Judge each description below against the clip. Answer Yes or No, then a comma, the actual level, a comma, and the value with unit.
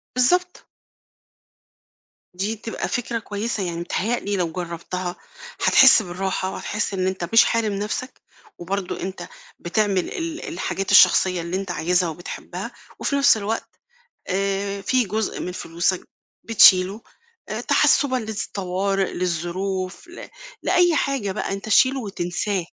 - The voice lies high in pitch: Yes, high, 195 Hz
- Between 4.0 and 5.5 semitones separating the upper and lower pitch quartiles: No, average, 3.6 semitones